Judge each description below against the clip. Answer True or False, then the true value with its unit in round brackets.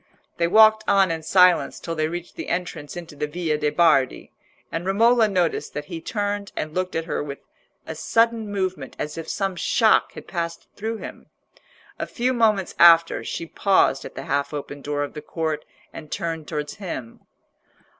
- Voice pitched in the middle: True (170 Hz)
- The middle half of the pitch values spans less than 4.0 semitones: False (4.4 semitones)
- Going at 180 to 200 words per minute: True (185 wpm)